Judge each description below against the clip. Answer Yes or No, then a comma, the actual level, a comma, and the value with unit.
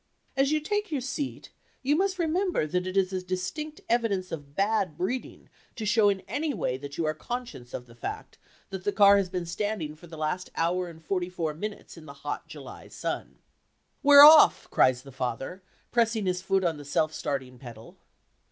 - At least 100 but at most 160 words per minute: No, average, 195 wpm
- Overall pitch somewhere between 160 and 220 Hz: Yes, medium, 185 Hz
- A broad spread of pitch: Yes, wide, 7.2 semitones